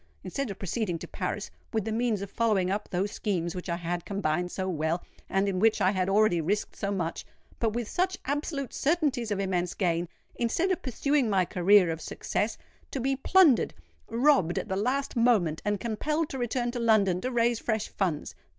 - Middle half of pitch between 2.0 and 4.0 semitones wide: No, average, 4.9 semitones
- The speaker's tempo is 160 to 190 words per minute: Yes, average, 180 wpm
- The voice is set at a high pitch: Yes, high, 210 Hz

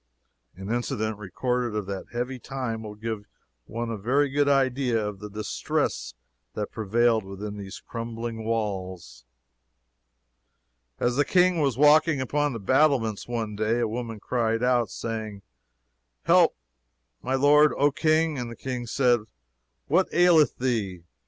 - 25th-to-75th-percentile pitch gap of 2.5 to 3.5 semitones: No, average, 4.0 semitones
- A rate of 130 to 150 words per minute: Yes, average, 140 wpm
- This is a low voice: Yes, low, 115 Hz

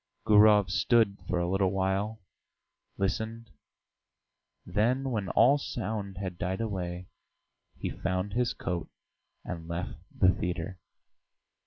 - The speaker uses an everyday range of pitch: Yes, average, 3.2 semitones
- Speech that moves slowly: Yes, slow, 115 wpm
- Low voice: Yes, very low, 95 Hz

